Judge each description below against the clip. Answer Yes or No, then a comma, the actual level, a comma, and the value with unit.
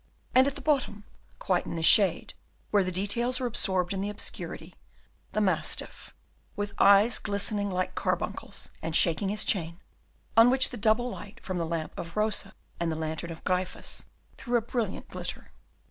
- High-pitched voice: Yes, high, 200 Hz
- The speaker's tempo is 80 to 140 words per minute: No, average, 175 wpm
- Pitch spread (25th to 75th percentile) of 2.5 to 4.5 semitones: Yes, average, 3.6 semitones